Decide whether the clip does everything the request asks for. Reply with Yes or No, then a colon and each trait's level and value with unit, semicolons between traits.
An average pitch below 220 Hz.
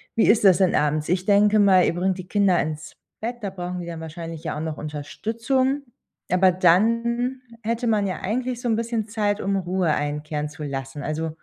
Yes: medium, 185 Hz